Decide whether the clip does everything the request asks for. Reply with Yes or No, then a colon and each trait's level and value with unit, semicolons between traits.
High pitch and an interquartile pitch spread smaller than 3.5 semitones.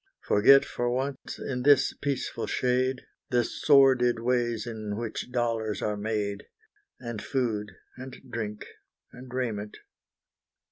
No: low, 120 Hz; average, 2.9 semitones